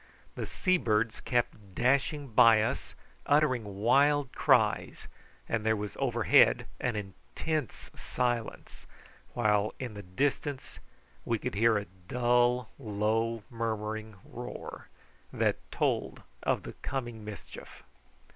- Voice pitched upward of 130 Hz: No, low, 115 Hz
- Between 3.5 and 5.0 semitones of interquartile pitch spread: No, average, 2.9 semitones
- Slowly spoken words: Yes, slow, 115 wpm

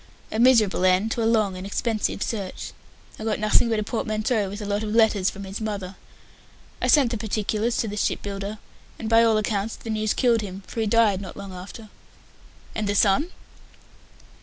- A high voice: Yes, high, 215 Hz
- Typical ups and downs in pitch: No, narrow, 2.1 semitones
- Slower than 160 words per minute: No, average, 200 wpm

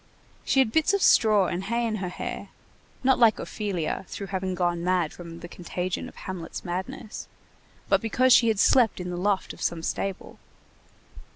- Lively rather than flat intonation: No, average, 4.0 semitones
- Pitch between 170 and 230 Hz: Yes, high, 190 Hz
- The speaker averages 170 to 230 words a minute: Yes, average, 180 wpm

